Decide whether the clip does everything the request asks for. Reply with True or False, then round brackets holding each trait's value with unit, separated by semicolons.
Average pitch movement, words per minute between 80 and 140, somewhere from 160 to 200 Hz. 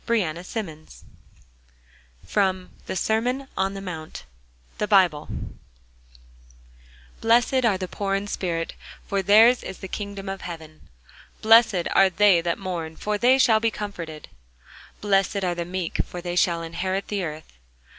True (3.4 semitones; 135 wpm; 190 Hz)